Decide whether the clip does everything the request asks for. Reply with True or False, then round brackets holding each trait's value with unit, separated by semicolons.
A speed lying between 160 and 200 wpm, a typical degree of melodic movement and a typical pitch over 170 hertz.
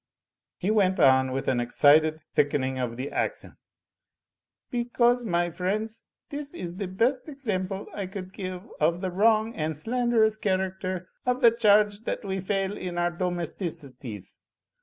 False (145 wpm; 4.9 semitones; 185 Hz)